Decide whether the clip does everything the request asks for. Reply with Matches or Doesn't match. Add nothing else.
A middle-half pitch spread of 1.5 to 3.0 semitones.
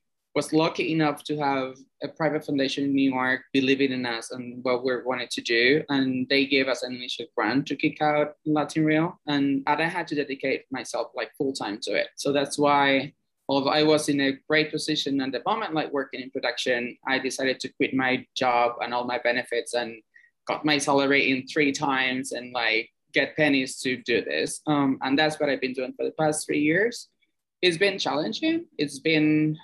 Matches